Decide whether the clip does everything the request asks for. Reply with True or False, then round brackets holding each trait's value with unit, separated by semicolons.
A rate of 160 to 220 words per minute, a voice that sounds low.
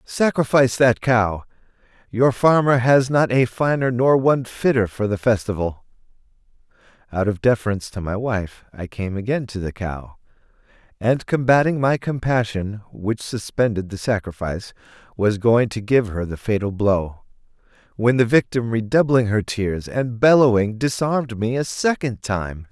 False (150 wpm; 115 Hz)